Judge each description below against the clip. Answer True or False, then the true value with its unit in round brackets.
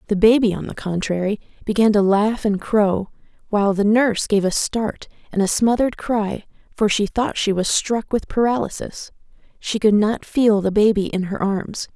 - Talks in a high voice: True (210 Hz)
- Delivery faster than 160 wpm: True (185 wpm)